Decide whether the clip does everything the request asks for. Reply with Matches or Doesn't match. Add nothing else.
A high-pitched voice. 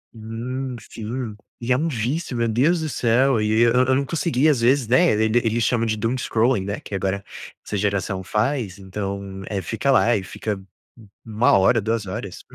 Doesn't match